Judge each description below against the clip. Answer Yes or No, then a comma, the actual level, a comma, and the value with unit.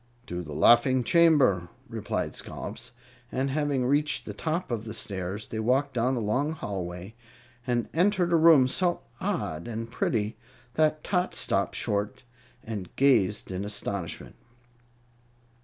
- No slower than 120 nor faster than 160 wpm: Yes, average, 145 wpm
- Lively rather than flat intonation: Yes, wide, 6.7 semitones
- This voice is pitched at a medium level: No, low, 120 Hz